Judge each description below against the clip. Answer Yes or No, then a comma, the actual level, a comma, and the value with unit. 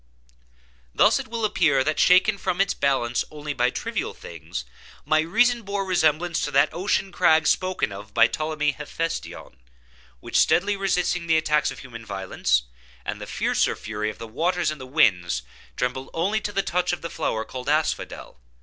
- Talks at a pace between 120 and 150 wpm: No, average, 175 wpm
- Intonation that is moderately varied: No, wide, 6.2 semitones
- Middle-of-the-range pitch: Yes, medium, 155 Hz